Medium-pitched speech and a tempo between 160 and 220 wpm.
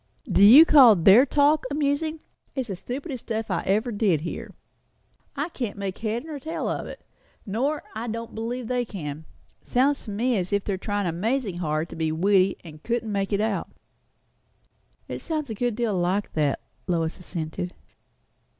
No: high, 215 Hz; average, 175 wpm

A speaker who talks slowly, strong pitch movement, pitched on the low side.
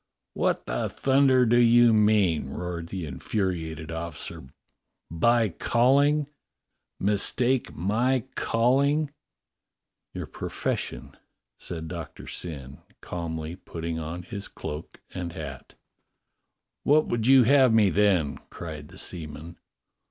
Yes: slow, 115 wpm; wide, 6.8 semitones; very low, 95 Hz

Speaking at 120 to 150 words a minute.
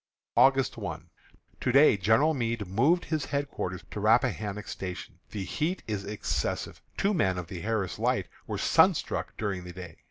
No: average, 160 wpm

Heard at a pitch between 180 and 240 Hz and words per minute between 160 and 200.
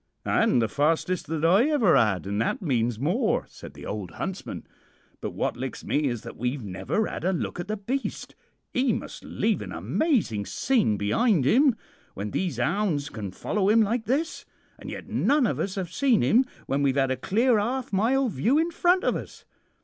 Yes: medium, 185 Hz; average, 195 wpm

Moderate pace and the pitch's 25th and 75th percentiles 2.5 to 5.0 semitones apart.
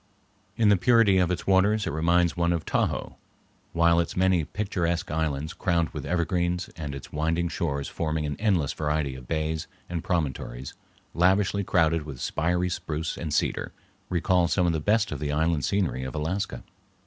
Yes: average, 170 wpm; average, 2.9 semitones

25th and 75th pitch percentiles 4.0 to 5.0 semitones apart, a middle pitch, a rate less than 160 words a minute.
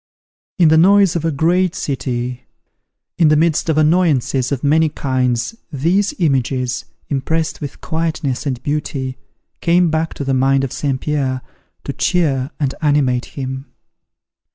No: average, 3.6 semitones; medium, 145 Hz; average, 145 wpm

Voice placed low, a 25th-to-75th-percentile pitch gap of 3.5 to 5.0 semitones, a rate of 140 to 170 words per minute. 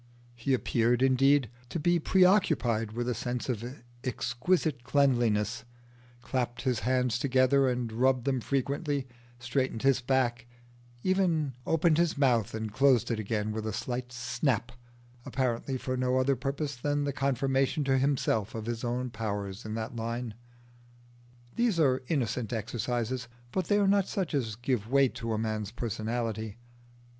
No: low, 125 Hz; average, 3.0 semitones; average, 155 wpm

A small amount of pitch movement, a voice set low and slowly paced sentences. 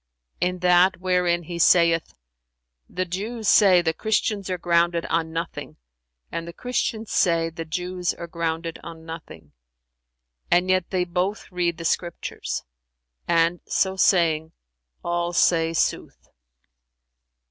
No: narrow, 1.7 semitones; medium, 175 Hz; slow, 125 wpm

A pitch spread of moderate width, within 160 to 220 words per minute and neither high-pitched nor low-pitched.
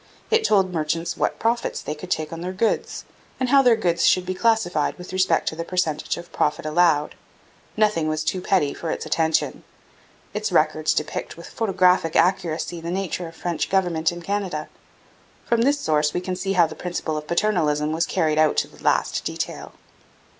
Yes: average, 3.4 semitones; average, 190 wpm; medium, 175 Hz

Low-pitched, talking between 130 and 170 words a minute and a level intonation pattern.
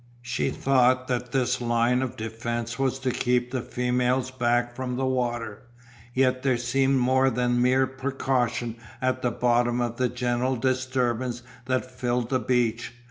Yes: low, 125 Hz; average, 155 wpm; narrow, 1.2 semitones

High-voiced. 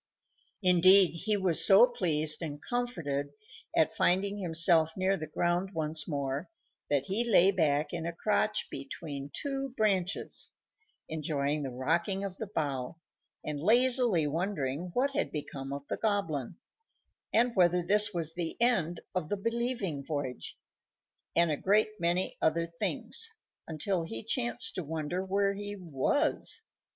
No: medium, 175 Hz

